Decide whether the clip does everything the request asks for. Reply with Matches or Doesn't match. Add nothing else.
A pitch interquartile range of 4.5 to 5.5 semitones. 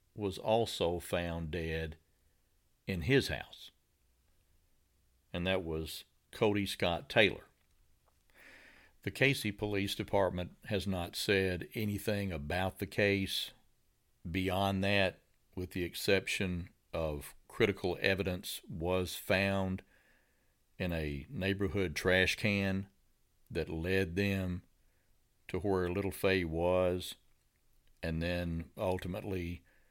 Doesn't match